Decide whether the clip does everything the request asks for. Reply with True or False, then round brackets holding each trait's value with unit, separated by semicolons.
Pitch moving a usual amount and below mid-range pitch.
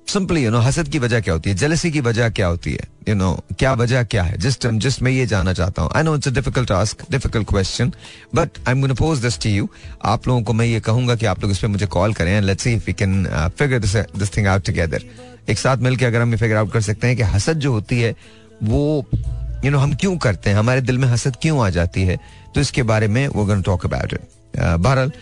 True (4.3 semitones; 115 Hz)